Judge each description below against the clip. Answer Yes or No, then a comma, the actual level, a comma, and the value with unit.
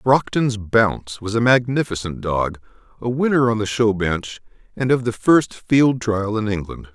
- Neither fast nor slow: Yes, average, 175 wpm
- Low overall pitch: Yes, low, 110 Hz